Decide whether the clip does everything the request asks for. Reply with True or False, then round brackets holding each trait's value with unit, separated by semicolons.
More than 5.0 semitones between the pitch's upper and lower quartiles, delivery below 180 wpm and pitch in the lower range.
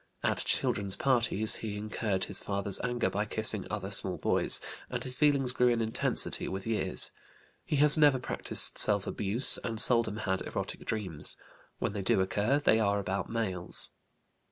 False (3.5 semitones; 165 wpm; 105 Hz)